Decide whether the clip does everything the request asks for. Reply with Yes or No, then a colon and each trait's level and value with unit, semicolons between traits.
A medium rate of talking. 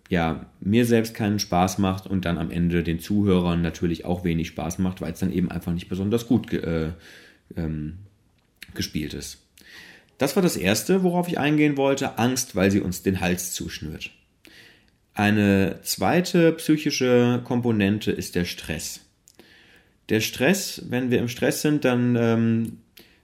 Yes: average, 160 wpm